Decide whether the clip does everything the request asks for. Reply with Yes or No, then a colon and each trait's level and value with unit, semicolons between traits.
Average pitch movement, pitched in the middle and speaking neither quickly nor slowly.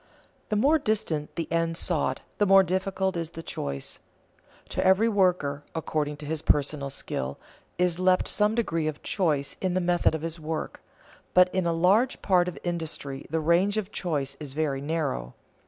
Yes: average, 3.9 semitones; medium, 165 Hz; average, 175 wpm